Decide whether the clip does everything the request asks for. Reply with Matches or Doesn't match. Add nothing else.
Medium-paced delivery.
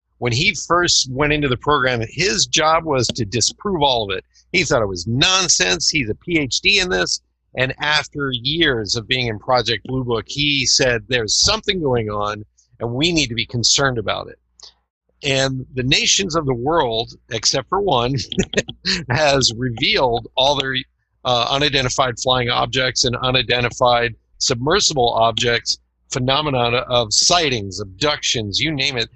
Matches